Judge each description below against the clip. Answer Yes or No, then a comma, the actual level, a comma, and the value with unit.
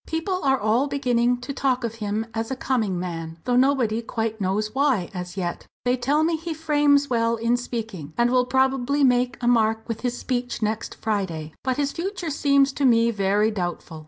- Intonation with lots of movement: No, average, 4.0 semitones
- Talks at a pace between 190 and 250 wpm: Yes, average, 195 wpm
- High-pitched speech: Yes, high, 240 Hz